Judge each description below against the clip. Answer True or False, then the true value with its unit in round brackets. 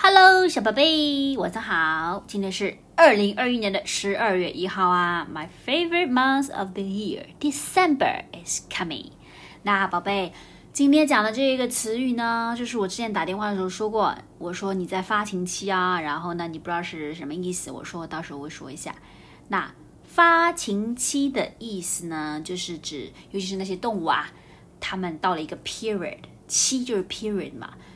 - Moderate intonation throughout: False (5.7 semitones)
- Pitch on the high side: True (200 Hz)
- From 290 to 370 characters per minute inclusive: True (345 characters per minute)